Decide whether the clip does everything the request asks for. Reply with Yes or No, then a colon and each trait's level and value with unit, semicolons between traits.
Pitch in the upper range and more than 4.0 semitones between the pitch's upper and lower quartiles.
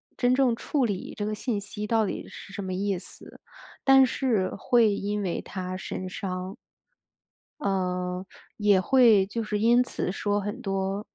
No: high, 205 Hz; average, 3.2 semitones